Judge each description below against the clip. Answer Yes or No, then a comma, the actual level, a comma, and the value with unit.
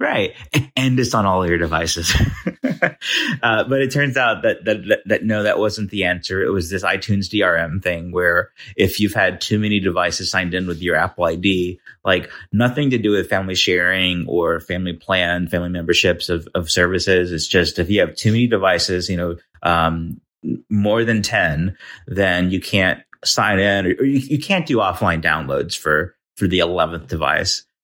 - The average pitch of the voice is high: No, very low, 95 Hz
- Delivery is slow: No, average, 190 wpm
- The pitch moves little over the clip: No, average, 3.0 semitones